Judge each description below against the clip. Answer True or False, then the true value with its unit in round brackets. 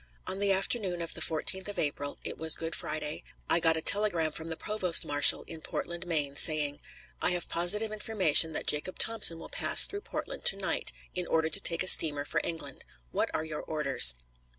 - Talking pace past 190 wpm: True (200 wpm)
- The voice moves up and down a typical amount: True (3.5 semitones)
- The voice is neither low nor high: True (165 Hz)